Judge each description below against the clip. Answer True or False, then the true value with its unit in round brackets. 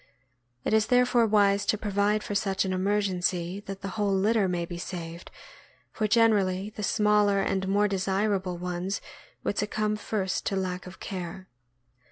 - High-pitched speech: True (195 Hz)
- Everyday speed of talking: True (160 wpm)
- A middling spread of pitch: False (2.0 semitones)